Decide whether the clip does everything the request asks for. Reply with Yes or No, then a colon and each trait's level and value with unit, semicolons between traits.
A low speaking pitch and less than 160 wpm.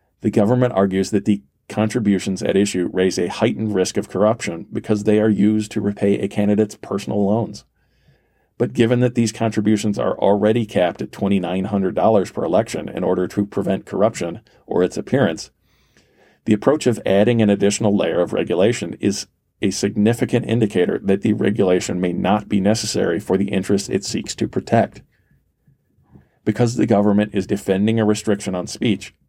No: low, 105 Hz; average, 165 wpm